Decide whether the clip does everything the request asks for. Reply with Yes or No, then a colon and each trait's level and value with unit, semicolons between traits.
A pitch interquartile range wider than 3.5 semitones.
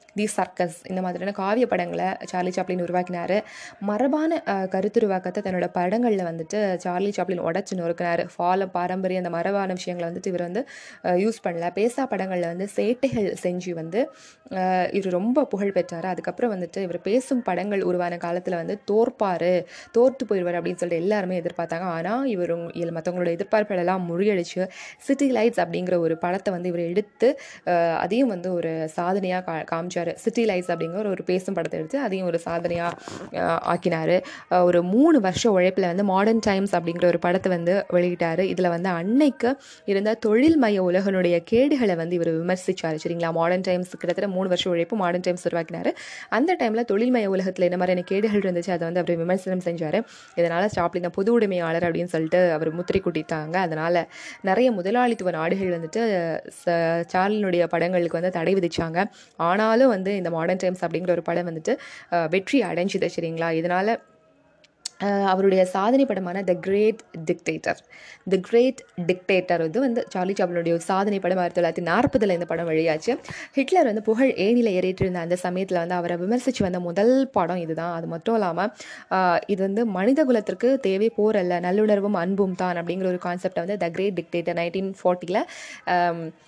No: average, 3.1 semitones